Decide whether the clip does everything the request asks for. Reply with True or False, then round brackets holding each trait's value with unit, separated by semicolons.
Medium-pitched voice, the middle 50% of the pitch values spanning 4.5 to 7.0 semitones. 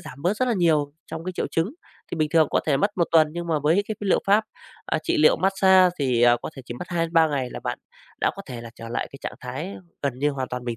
True (160 Hz; 5.0 semitones)